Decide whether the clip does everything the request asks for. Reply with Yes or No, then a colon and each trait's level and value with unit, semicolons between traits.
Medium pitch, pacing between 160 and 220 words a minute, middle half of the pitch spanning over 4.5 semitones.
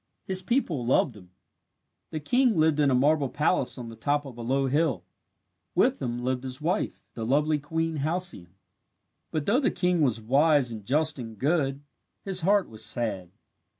Yes: medium, 145 Hz; average, 180 wpm; average, 5.0 semitones